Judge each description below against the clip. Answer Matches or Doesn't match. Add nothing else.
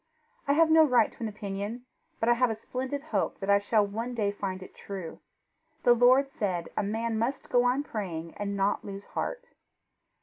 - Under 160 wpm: Doesn't match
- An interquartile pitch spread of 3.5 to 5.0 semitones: Matches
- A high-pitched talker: Matches